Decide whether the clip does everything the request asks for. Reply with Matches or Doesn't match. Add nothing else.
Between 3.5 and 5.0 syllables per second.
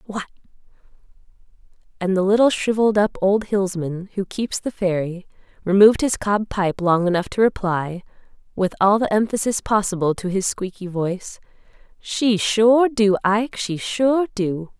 Matches